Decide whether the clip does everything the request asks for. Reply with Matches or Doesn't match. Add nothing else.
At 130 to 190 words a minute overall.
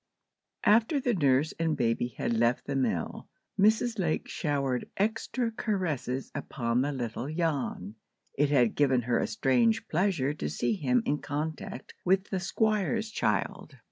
Matches